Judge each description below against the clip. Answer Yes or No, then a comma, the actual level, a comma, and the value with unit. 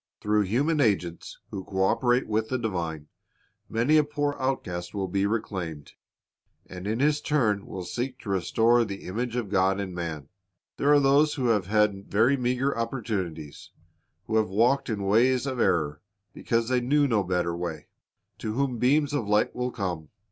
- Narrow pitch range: No, average, 5.2 semitones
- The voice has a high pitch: No, low, 110 Hz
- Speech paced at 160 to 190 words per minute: Yes, average, 175 wpm